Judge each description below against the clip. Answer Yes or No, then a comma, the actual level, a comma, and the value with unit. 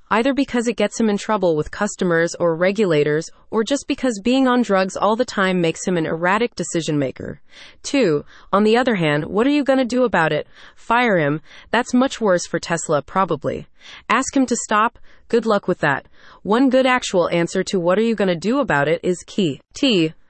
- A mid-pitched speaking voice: No, high, 200 Hz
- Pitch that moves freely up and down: Yes, wide, 6.2 semitones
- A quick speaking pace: Yes, fast, 210 wpm